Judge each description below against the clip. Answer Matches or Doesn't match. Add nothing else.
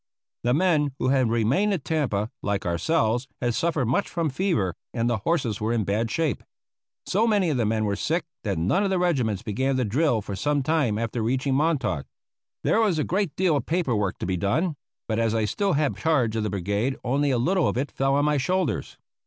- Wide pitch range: Matches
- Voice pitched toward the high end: Doesn't match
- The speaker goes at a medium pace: Doesn't match